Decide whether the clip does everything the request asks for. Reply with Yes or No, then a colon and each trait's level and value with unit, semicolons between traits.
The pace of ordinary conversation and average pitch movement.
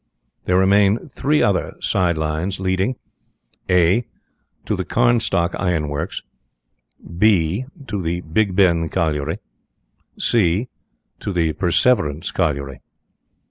No: slow, 105 wpm; average, 3.7 semitones